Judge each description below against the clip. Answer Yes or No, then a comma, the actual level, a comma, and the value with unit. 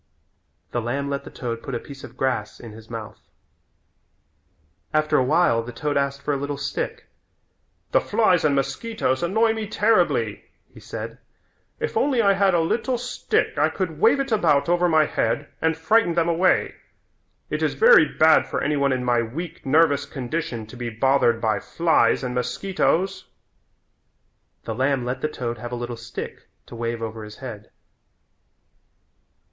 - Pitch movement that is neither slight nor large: No, wide, 6.3 semitones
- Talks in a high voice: No, medium, 140 Hz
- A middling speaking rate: Yes, average, 170 wpm